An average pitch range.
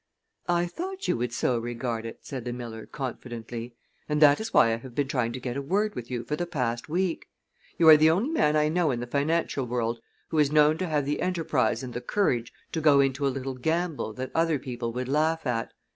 Yes: average, 4.8 semitones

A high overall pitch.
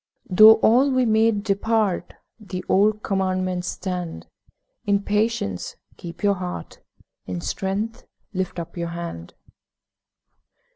Yes: high, 195 Hz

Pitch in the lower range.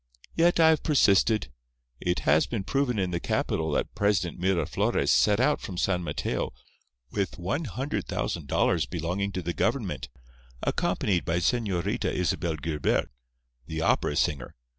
Yes: very low, 95 Hz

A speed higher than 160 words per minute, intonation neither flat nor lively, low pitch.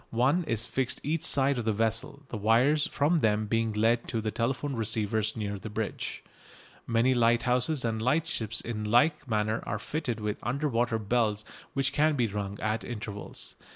Yes: average, 170 wpm; average, 3.4 semitones; low, 115 Hz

